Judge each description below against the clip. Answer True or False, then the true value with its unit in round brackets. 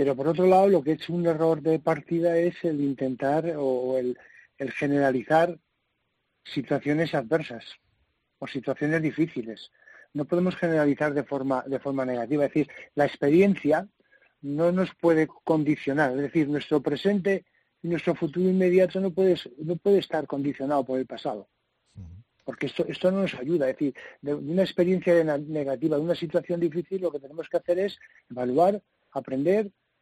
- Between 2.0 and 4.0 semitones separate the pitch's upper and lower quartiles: True (3.7 semitones)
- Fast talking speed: False (160 wpm)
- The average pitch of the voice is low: False (155 Hz)